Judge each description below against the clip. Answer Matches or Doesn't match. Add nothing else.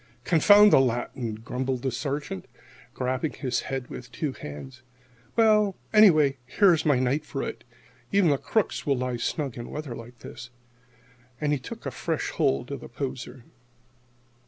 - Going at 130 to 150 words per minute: Doesn't match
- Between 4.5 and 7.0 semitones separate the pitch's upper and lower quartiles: Doesn't match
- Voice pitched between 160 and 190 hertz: Doesn't match